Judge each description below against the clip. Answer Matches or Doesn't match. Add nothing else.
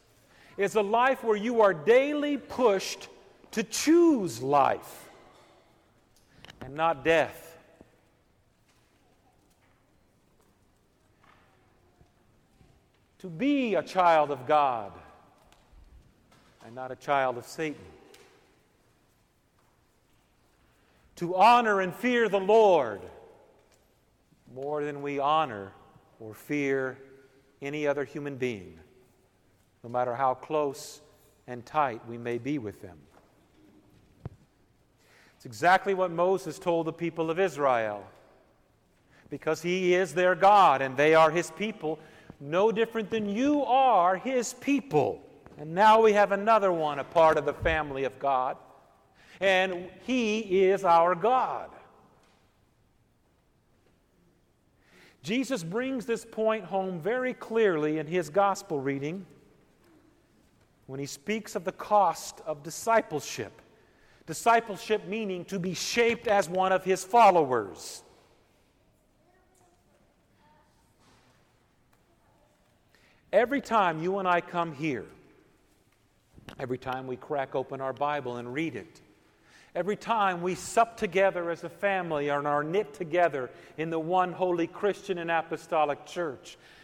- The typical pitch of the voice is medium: Matches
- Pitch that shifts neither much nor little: Doesn't match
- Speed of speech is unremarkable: Doesn't match